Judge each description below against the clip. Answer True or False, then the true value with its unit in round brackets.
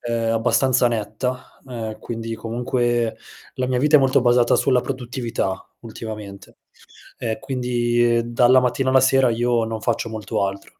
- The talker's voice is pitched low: True (120 Hz)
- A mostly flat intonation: True (2.0 semitones)